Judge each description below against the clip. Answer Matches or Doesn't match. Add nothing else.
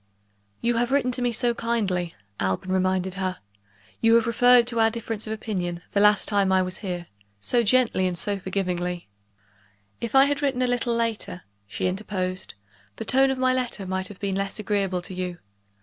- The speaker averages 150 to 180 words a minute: Doesn't match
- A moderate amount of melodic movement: Matches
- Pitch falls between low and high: Doesn't match